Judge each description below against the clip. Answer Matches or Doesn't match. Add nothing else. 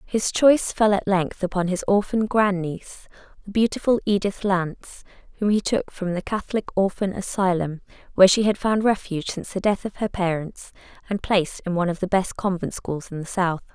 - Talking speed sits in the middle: Matches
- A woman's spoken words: Matches